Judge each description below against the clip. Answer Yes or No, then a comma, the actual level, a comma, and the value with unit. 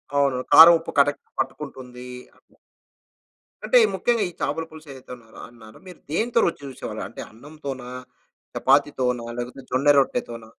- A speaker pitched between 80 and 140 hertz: Yes, low, 135 Hz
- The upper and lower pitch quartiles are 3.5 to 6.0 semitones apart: Yes, average, 4.0 semitones